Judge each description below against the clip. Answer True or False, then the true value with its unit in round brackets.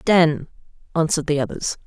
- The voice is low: False (155 Hz)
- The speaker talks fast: False (130 wpm)